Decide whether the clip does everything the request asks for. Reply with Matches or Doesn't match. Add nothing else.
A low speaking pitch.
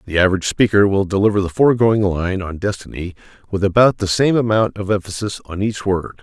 Matches